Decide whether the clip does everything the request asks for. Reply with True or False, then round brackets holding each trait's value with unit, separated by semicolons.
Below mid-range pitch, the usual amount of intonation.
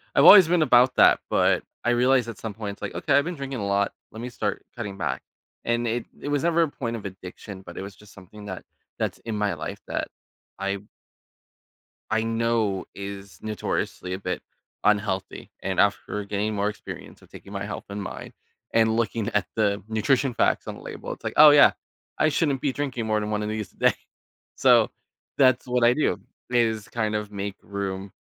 True (110 Hz; 3.4 semitones)